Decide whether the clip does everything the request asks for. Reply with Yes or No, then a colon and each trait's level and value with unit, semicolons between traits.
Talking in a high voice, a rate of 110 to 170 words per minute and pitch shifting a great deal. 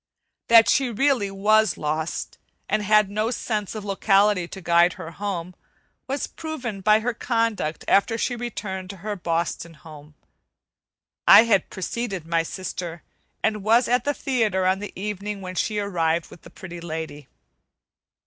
No: high, 200 Hz; average, 155 wpm; average, 4.3 semitones